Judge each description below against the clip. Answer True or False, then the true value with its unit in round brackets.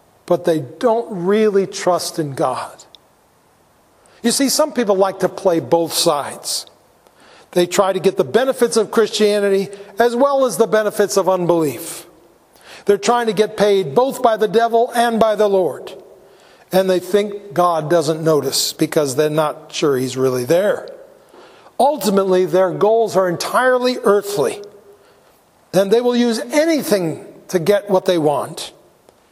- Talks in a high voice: True (200 Hz)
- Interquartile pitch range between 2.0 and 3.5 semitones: False (4.8 semitones)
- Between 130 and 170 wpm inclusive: True (150 wpm)